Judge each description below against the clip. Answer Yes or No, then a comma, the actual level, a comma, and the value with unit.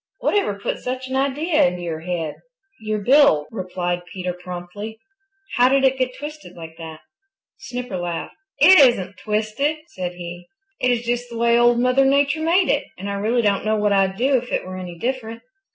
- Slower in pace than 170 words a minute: No, average, 190 wpm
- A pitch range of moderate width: No, wide, 6.2 semitones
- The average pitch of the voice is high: Yes, high, 220 Hz